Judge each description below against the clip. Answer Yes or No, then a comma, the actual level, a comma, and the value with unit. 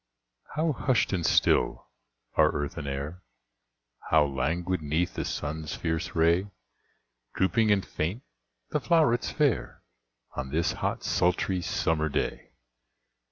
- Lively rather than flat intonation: No, average, 4.6 semitones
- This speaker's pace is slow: Yes, slow, 120 wpm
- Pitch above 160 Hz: No, very low, 85 Hz